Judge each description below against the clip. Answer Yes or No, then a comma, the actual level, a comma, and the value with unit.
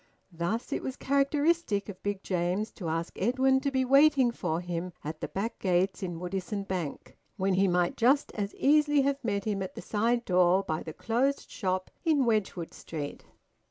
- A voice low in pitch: No, high, 200 Hz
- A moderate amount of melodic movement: No, wide, 6.6 semitones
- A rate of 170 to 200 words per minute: Yes, average, 185 wpm